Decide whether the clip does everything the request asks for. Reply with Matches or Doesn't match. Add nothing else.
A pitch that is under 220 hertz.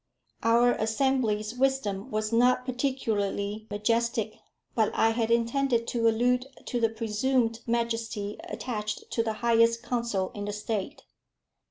Doesn't match